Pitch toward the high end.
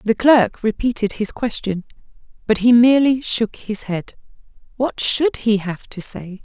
Yes: high, 225 Hz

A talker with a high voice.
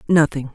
No: medium, 150 Hz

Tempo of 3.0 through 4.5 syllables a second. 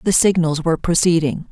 No: 5.8 syllables/s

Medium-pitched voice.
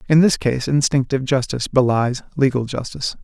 No: low, 130 Hz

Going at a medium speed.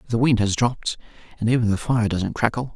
Yes: average, 195 wpm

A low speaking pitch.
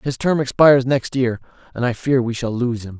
Yes: low, 125 Hz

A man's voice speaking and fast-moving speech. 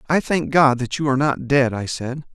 Yes: male; fast, 255 wpm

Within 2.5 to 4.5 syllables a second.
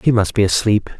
No: 5.3 syllables/s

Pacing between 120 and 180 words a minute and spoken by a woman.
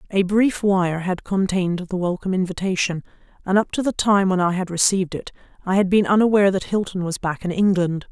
No: fast, 205 wpm; female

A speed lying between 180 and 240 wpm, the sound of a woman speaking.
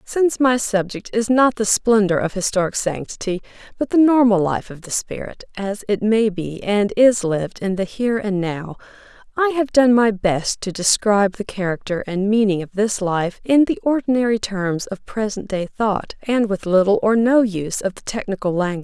Yes: average, 200 wpm; female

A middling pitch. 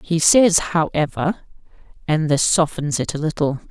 Yes: medium, 160 Hz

